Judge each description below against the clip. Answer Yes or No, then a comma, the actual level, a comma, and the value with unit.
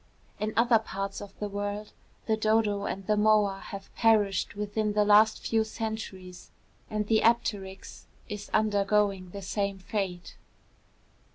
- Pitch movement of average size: No, narrow, 1.6 semitones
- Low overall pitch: No, high, 210 Hz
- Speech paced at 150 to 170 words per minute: No, average, 140 wpm